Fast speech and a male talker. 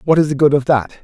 Yes: fast, 350 wpm; male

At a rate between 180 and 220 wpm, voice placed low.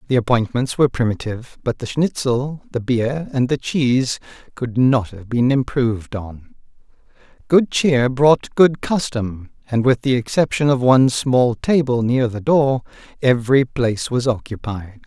No: average, 150 wpm; low, 125 Hz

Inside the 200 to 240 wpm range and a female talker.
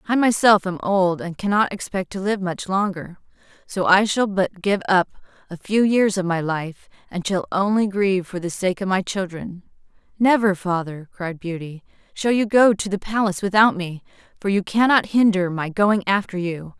No: average, 190 wpm; female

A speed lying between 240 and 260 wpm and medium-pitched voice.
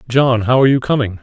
No: fast, 245 wpm; low, 120 Hz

